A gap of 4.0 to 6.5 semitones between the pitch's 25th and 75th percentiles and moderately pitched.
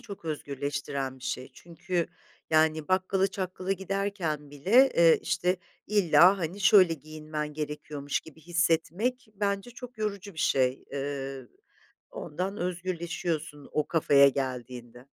Yes: average, 5.0 semitones; medium, 165 Hz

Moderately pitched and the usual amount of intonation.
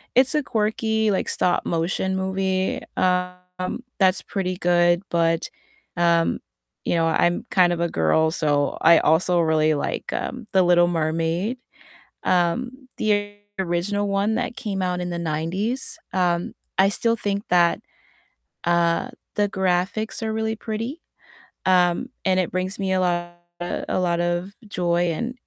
Yes: medium, 180 Hz; average, 3.0 semitones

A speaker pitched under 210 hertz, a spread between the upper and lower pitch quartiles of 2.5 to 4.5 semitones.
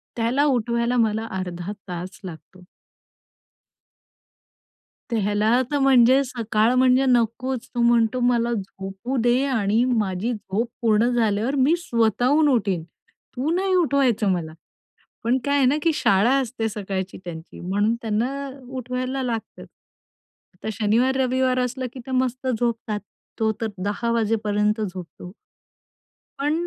No: high, 235 Hz; average, 3.7 semitones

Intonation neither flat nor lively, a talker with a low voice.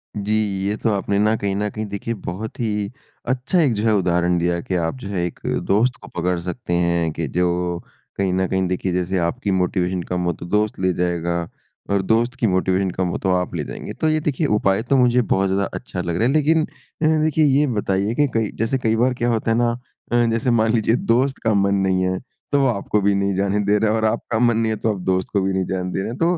Yes: average, 4.0 semitones; low, 100 Hz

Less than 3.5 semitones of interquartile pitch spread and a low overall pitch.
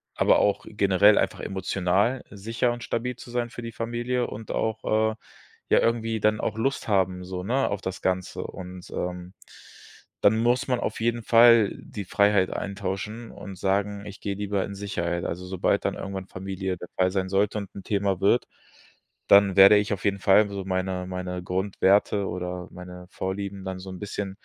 Yes: narrow, 2.5 semitones; low, 100 Hz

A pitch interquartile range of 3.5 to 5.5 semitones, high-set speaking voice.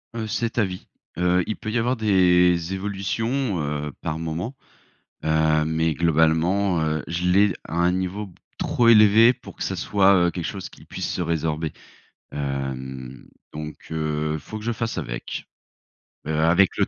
No: average, 4.5 semitones; very low, 90 Hz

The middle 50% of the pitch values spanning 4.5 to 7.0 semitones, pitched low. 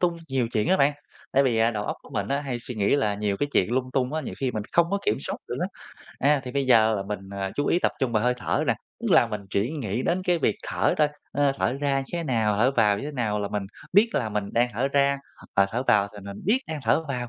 Yes: average, 4.9 semitones; low, 125 Hz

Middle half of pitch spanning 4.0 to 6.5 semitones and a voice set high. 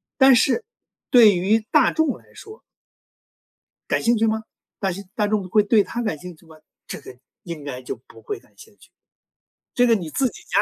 Yes: average, 5.3 semitones; high, 215 Hz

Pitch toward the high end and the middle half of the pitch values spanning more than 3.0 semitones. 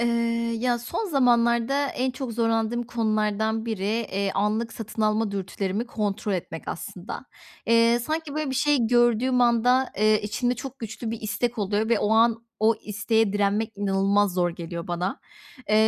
No: high, 225 Hz; average, 2.7 semitones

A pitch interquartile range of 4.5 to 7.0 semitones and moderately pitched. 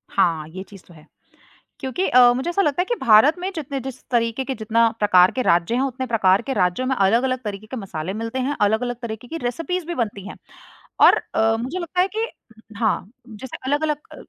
No: average, 4.8 semitones; high, 240 Hz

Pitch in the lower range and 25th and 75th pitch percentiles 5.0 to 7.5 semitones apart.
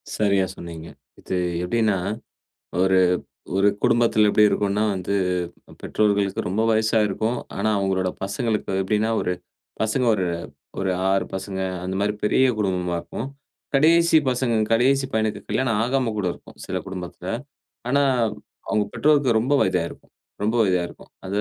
No: low, 105 Hz; average, 3.4 semitones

